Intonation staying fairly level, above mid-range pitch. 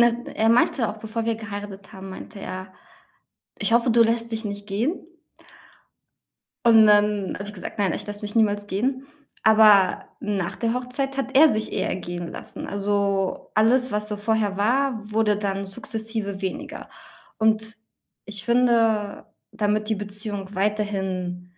Yes: narrow, 2.2 semitones; high, 210 Hz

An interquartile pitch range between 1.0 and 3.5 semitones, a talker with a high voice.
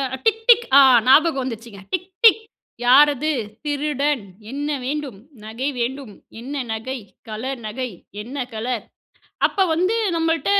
No: average, 4.0 semitones; very high, 275 Hz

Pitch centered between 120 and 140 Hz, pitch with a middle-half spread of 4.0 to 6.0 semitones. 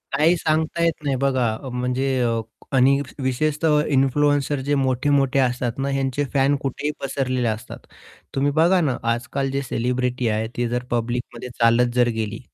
No: low, 135 Hz; average, 2.7 semitones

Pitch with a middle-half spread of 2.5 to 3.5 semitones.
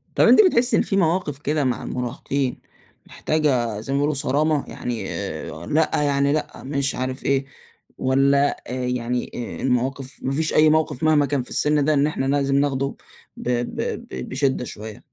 Yes: average, 2.8 semitones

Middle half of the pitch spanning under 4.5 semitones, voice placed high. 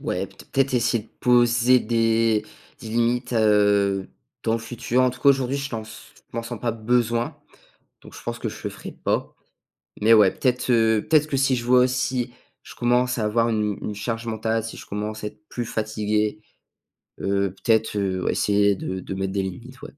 No: narrow, 2.6 semitones; low, 115 Hz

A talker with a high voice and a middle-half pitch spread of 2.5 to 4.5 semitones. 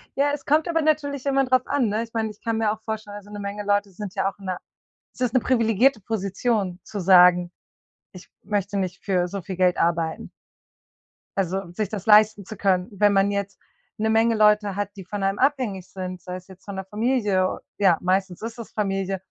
Yes: high, 205 Hz; average, 2.9 semitones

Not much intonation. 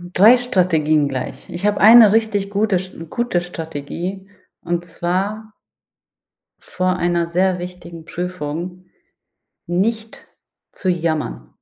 No: average, 3.0 semitones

